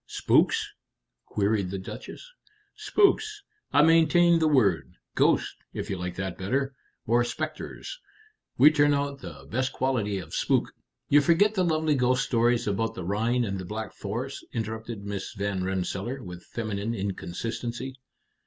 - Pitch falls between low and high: No, low, 120 Hz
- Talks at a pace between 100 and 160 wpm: Yes, average, 150 wpm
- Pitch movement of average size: No, wide, 6.3 semitones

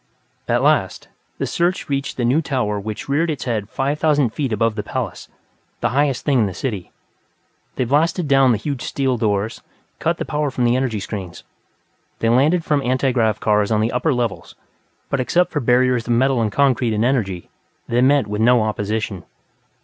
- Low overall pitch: Yes, low, 125 Hz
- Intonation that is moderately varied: Yes, average, 4.1 semitones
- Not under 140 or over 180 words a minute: No, average, 190 wpm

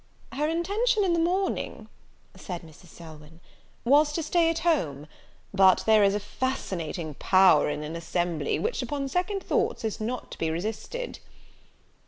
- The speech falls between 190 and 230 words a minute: No, average, 155 wpm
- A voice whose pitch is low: No, high, 220 Hz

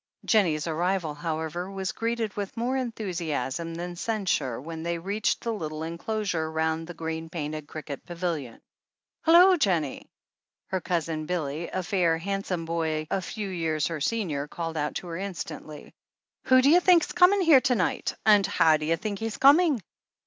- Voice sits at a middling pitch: Yes, medium, 175 Hz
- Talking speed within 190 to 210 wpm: No, average, 170 wpm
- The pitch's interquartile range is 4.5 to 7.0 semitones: Yes, average, 4.9 semitones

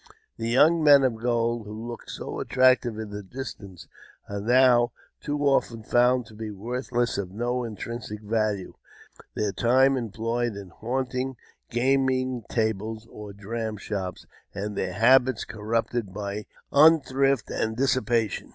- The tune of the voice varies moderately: Yes, average, 3.2 semitones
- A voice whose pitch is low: Yes, low, 115 Hz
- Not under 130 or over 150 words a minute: Yes, average, 145 wpm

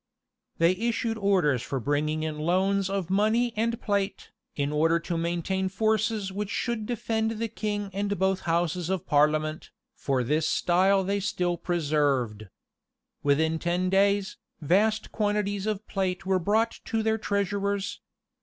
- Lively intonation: No, average, 4.2 semitones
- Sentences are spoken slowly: No, average, 145 wpm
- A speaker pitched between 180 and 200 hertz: Yes, high, 190 Hz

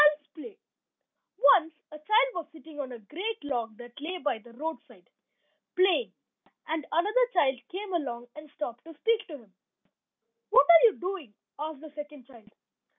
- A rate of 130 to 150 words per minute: No, average, 165 wpm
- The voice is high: Yes, very high, 305 Hz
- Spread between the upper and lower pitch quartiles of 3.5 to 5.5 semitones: Yes, average, 5.2 semitones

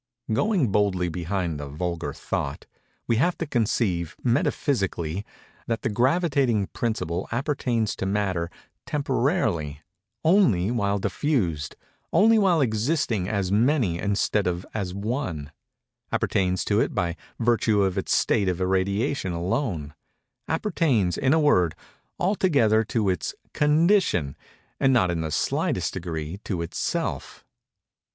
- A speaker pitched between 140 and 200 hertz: No, low, 105 Hz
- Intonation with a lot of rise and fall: Yes, wide, 6.8 semitones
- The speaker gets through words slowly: Yes, slow, 115 wpm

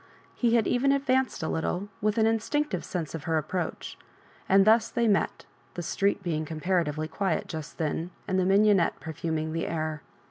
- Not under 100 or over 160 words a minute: No, average, 170 wpm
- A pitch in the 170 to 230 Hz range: Yes, medium, 185 Hz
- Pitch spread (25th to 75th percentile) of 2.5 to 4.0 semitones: No, wide, 5.4 semitones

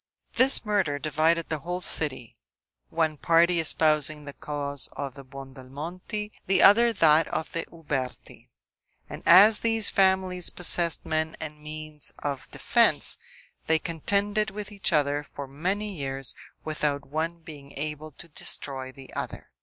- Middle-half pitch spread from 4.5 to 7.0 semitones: No, average, 4.1 semitones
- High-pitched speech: No, medium, 155 Hz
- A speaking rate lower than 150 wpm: Yes, average, 140 wpm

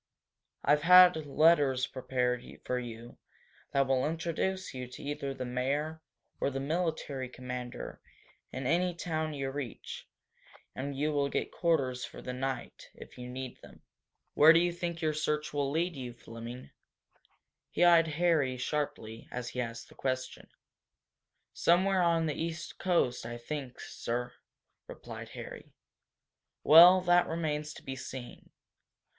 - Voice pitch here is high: No, medium, 140 Hz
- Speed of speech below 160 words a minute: Yes, average, 145 wpm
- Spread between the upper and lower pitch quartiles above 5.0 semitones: No, average, 4.5 semitones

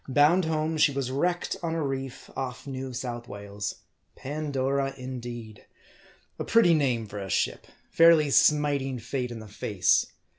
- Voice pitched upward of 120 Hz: Yes, low, 135 Hz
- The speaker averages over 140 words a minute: Yes, average, 150 wpm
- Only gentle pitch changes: No, average, 3.9 semitones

